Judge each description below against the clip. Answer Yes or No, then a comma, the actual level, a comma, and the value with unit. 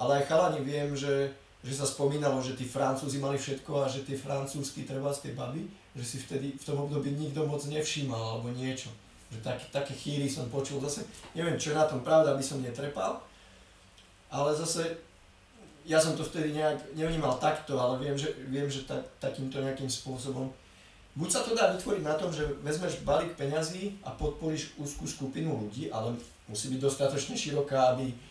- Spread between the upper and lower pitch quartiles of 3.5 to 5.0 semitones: No, narrow, 2.4 semitones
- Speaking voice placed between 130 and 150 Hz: Yes, medium, 140 Hz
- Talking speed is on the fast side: Yes, fast, 185 wpm